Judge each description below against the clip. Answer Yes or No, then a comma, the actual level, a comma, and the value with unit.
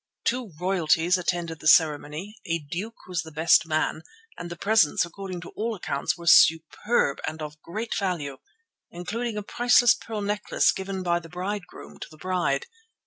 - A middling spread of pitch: Yes, average, 4.2 semitones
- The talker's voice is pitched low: No, medium, 175 Hz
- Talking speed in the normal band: Yes, average, 165 wpm